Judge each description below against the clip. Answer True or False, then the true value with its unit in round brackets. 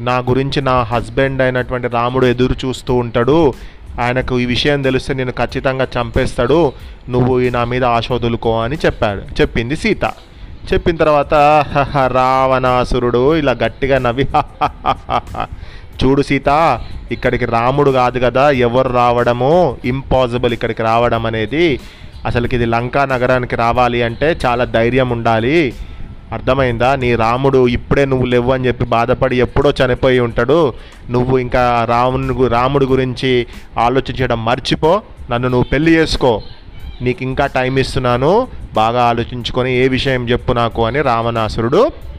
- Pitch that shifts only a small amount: True (1.7 semitones)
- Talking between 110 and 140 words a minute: True (125 wpm)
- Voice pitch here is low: True (125 Hz)